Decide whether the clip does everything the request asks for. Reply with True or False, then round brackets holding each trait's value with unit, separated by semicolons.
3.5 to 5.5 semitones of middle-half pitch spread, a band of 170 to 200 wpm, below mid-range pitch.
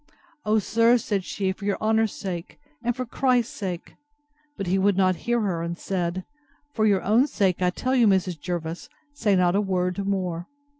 False (4.4 semitones; 180 wpm; 200 Hz)